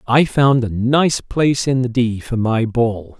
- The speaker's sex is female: No, male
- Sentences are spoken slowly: No, fast, 205 wpm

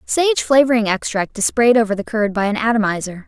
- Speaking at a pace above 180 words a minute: Yes, average, 200 wpm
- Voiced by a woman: Yes, female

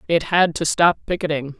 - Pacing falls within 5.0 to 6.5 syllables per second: Yes, 5.2 syllables/s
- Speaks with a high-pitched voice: No, medium, 165 Hz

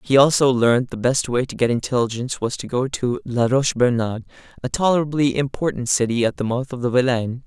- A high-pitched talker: No, low, 125 Hz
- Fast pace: Yes, fast, 210 wpm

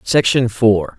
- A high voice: No, low, 110 Hz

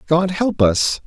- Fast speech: No, average, 170 wpm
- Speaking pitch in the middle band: Yes, medium, 165 Hz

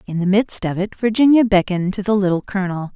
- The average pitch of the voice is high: Yes, high, 195 Hz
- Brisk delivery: Yes, fast, 225 wpm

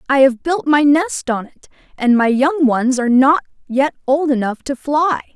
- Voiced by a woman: Yes, female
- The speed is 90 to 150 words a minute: No, average, 200 wpm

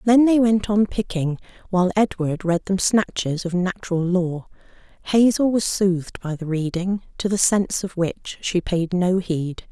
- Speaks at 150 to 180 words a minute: Yes, average, 175 wpm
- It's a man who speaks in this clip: No, female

